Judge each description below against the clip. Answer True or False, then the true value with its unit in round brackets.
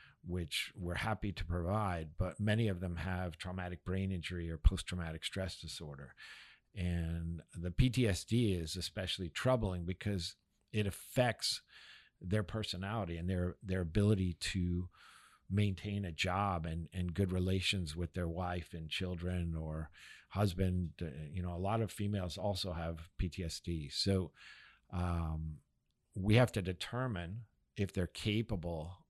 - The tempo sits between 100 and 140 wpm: True (135 wpm)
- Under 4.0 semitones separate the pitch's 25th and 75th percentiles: True (2.9 semitones)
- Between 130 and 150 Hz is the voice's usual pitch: False (90 Hz)